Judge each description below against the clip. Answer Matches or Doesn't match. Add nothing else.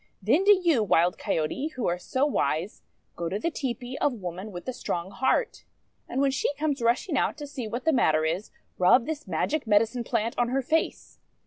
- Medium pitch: Doesn't match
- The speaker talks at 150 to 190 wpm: Doesn't match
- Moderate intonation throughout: Doesn't match